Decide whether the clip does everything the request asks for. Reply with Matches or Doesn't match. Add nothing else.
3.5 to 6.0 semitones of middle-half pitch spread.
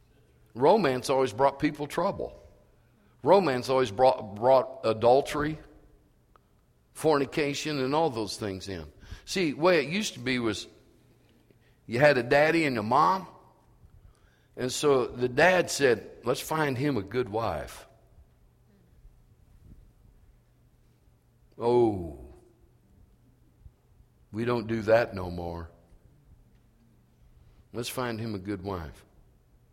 Matches